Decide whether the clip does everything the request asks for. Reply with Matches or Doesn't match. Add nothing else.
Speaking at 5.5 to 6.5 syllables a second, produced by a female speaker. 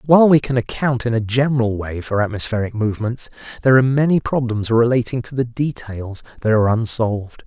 Doesn't match